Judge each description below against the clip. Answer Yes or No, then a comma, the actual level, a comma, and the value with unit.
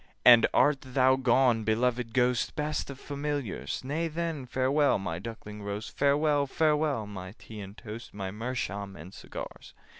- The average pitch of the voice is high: No, low, 125 Hz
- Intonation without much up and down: No, average, 5.1 semitones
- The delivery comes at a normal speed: Yes, average, 150 wpm